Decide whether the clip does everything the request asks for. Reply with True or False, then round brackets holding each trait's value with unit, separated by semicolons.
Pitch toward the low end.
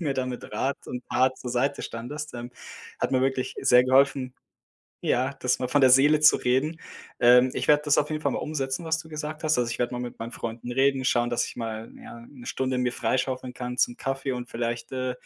True (130 Hz)